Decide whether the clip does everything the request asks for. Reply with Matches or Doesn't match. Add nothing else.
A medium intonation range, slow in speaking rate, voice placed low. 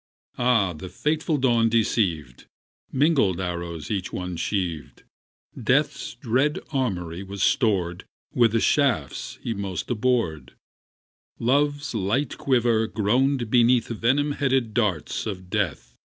Doesn't match